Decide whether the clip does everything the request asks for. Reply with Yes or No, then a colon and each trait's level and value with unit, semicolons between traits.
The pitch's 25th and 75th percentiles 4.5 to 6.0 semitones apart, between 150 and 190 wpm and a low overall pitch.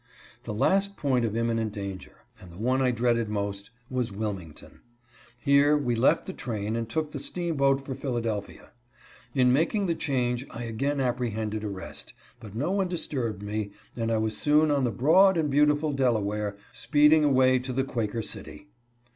Yes: average, 4.9 semitones; average, 170 wpm; low, 125 Hz